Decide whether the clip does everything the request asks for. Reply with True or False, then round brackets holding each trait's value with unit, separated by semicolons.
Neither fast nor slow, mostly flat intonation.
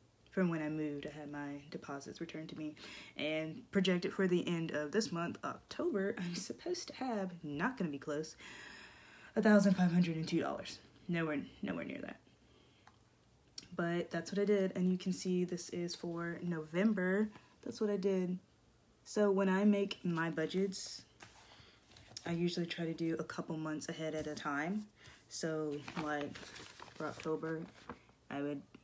False (165 wpm; 3.9 semitones)